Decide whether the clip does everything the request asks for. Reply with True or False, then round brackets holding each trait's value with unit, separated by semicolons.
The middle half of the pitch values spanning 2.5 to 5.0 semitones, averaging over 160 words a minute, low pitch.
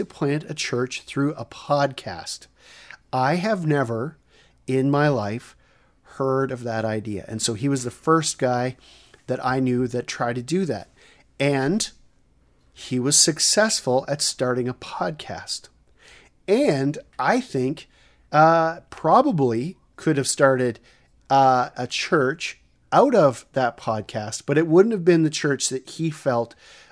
False (3.3 semitones; 145 wpm; 130 Hz)